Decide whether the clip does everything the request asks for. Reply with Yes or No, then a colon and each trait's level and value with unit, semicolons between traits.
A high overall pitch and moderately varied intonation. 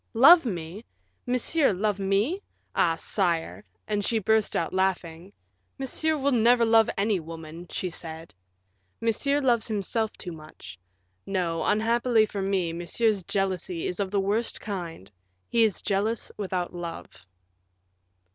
Yes: high, 200 Hz; average, 4.4 semitones